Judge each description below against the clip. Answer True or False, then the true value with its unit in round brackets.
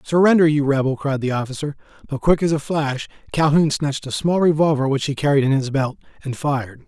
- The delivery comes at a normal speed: False (210 wpm)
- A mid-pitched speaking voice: True (145 Hz)